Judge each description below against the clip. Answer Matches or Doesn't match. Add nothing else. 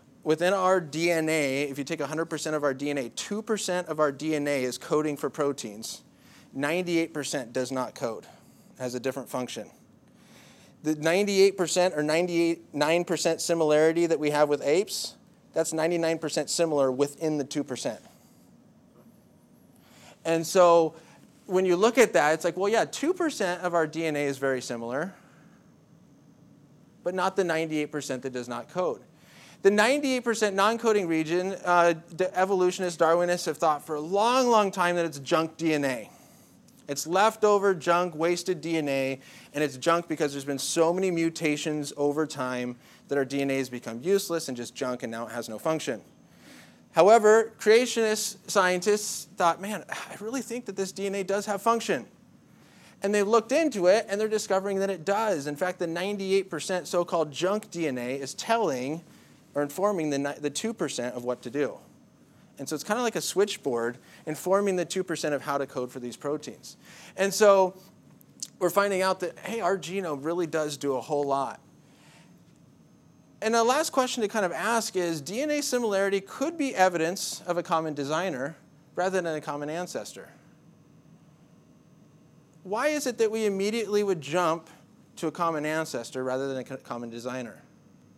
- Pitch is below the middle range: Doesn't match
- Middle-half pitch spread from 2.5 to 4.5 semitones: Doesn't match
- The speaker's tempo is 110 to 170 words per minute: Matches